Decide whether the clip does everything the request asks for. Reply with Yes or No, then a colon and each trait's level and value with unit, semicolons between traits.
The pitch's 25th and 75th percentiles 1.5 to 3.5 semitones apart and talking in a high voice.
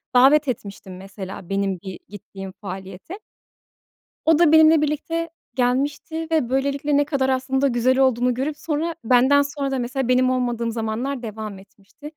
No: average, 4.8 semitones; very high, 255 Hz